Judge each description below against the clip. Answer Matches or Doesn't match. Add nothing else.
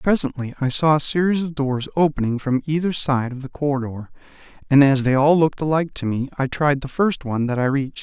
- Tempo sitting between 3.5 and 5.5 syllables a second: Doesn't match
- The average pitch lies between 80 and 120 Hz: Doesn't match